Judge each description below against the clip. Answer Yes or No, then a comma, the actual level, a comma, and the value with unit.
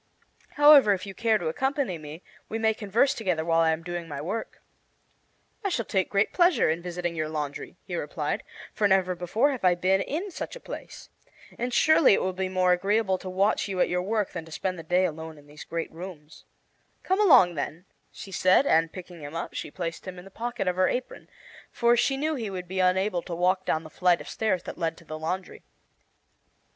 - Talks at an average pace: No, fast, 220 wpm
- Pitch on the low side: No, medium, 185 Hz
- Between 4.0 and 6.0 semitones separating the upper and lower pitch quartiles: Yes, average, 4.7 semitones